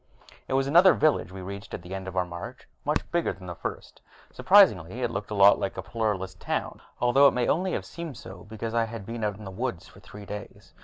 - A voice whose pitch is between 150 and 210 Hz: No, low, 105 Hz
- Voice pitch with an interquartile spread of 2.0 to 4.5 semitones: No, average, 5.0 semitones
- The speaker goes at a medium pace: No, fast, 245 wpm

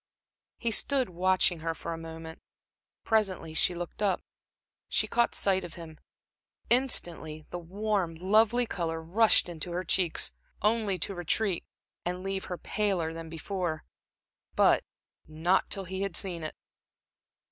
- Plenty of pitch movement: No, average, 3.5 semitones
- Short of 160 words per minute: Yes, average, 140 wpm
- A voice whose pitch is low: No, medium, 180 Hz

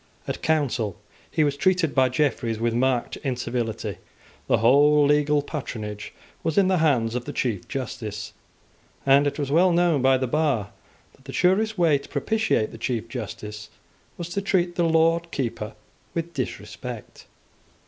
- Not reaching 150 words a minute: No, average, 160 wpm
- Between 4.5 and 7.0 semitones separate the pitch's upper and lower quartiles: Yes, wide, 5.6 semitones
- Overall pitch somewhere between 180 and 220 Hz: No, medium, 140 Hz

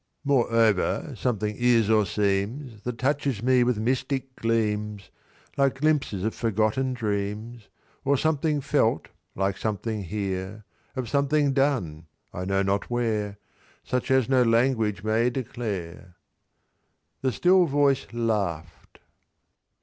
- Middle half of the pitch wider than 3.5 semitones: Yes, average, 4.3 semitones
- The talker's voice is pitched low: Yes, low, 115 Hz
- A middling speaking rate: No, slow, 120 wpm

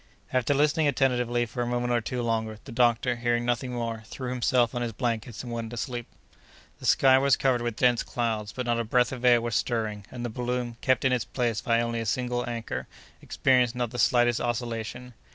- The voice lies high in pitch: No, low, 120 Hz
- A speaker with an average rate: No, fast, 210 wpm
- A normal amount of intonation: No, narrow, 1.2 semitones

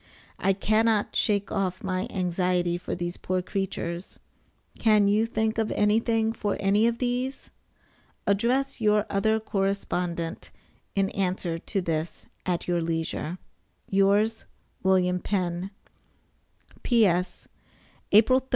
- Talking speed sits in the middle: No, slow, 115 wpm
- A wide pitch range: No, average, 3.4 semitones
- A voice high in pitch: Yes, high, 195 Hz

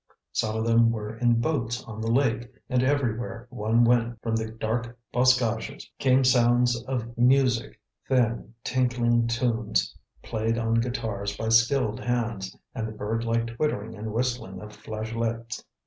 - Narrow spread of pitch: Yes, narrow, 1.6 semitones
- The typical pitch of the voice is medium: No, low, 115 Hz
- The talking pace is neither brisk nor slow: Yes, average, 145 wpm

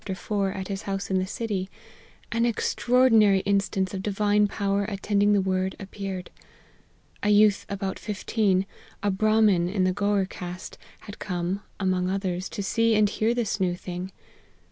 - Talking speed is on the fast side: No, average, 155 wpm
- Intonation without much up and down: Yes, narrow, 1.8 semitones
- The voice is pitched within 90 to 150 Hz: No, high, 200 Hz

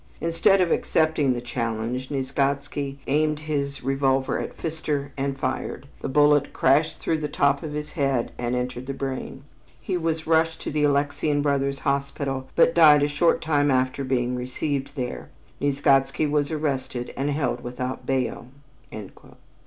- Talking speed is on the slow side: No, average, 155 wpm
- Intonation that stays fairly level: Yes, narrow, 2.2 semitones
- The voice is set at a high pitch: No, medium, 140 Hz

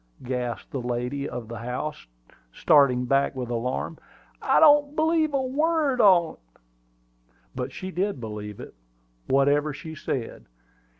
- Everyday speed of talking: No, slow, 130 wpm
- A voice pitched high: No, medium, 140 Hz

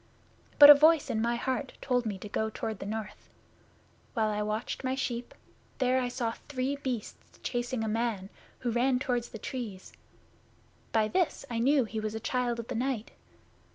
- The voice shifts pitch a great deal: No, average, 2.9 semitones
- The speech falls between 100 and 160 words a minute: No, average, 185 wpm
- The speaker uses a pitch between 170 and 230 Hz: No, high, 240 Hz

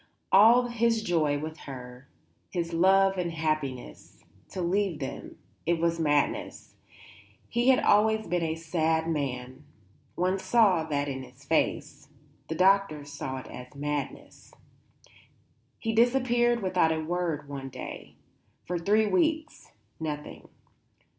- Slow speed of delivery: Yes, slow, 125 wpm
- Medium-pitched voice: Yes, medium, 165 Hz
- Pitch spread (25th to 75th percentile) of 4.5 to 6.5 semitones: Yes, average, 5.3 semitones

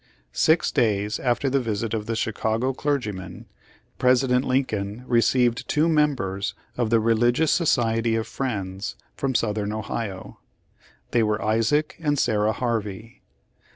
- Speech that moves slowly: Yes, slow, 130 wpm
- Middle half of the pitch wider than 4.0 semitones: No, average, 3.2 semitones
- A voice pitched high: No, low, 115 Hz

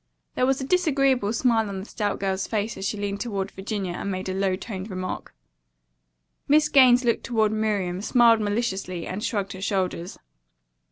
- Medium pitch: No, high, 205 Hz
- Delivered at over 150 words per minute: Yes, average, 175 wpm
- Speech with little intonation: No, average, 3.7 semitones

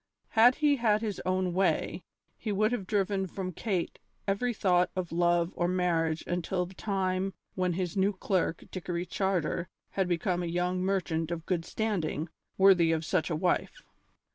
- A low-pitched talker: No, medium, 185 Hz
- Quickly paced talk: No, average, 165 wpm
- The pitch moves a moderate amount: No, narrow, 2.2 semitones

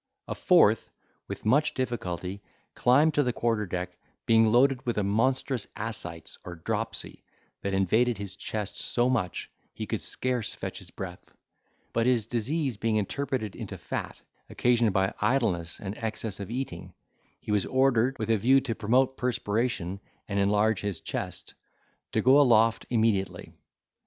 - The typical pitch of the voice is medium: No, low, 115 Hz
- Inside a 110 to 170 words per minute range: Yes, average, 150 wpm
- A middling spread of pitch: Yes, average, 4.0 semitones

